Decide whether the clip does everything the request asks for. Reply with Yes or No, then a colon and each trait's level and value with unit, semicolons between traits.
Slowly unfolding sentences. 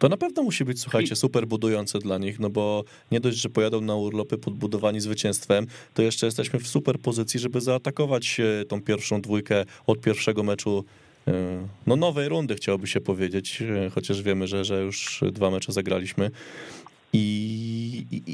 No: fast, 160 wpm